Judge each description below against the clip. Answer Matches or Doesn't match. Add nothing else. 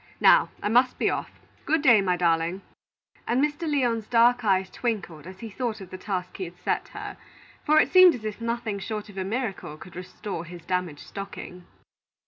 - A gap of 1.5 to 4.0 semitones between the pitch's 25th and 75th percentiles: Doesn't match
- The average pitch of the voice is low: Doesn't match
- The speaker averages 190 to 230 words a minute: Matches